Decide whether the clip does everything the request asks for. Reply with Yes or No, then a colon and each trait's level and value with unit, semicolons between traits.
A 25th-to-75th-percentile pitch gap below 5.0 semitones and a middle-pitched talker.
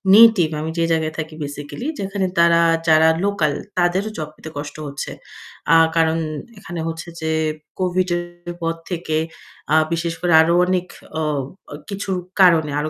Yes: narrow, 2.4 semitones; medium, 170 Hz